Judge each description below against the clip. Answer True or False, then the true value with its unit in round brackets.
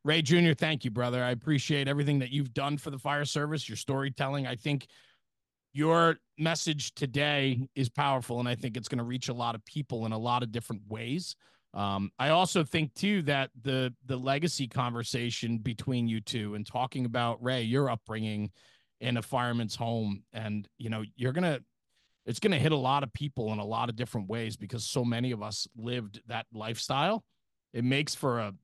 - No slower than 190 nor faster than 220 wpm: True (195 wpm)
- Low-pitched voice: True (125 Hz)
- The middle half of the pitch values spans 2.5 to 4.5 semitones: True (3.7 semitones)